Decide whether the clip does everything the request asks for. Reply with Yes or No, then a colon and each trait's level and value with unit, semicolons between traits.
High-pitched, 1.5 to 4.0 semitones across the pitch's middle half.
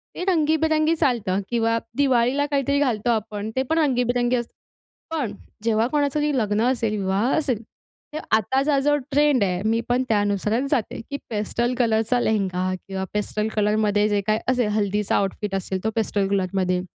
No: high, 225 Hz; average, 4.5 semitones